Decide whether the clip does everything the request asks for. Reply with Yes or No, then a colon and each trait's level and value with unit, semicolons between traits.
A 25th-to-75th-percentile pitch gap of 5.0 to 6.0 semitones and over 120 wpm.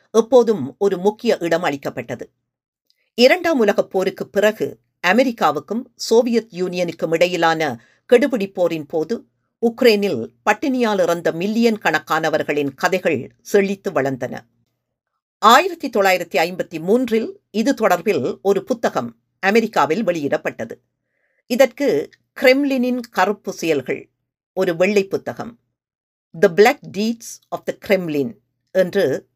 No: wide, 5.4 semitones; average, 100 wpm